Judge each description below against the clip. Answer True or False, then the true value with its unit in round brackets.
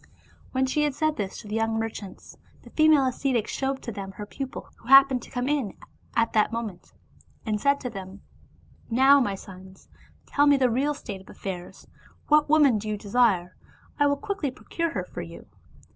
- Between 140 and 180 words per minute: False (205 wpm)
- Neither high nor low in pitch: False (245 Hz)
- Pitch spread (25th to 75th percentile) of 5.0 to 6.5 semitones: True (5.3 semitones)